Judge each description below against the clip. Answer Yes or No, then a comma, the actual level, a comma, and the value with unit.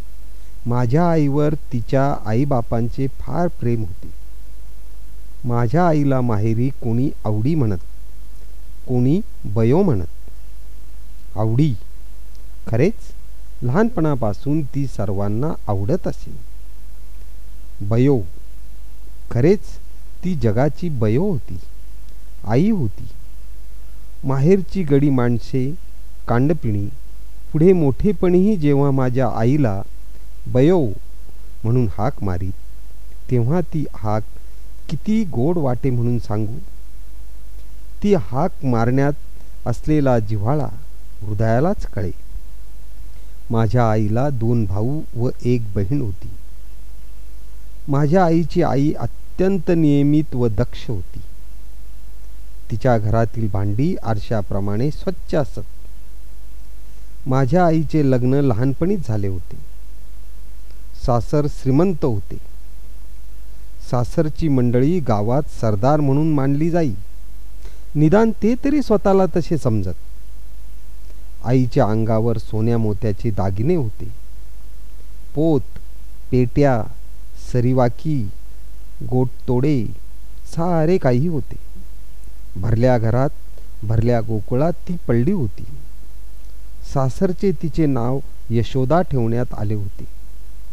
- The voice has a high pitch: No, low, 115 Hz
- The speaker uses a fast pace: No, average, 85 wpm